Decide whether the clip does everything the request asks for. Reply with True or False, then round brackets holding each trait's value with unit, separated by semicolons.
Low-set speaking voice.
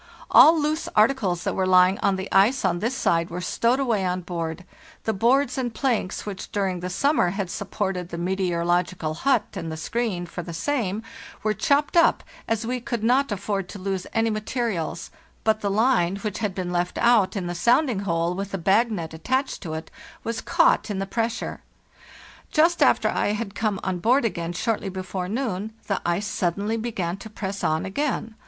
False (200 Hz)